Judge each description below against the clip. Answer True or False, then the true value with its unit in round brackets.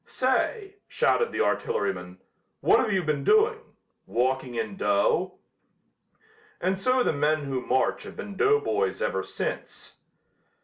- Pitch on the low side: False (190 Hz)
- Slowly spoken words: True (125 wpm)